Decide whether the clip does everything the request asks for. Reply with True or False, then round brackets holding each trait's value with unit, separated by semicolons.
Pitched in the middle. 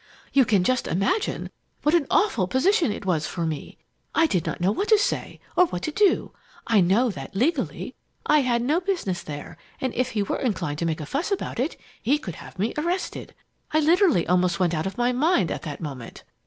False (235 Hz)